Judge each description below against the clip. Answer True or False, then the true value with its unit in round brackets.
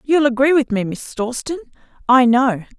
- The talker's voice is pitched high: True (255 Hz)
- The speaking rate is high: False (170 wpm)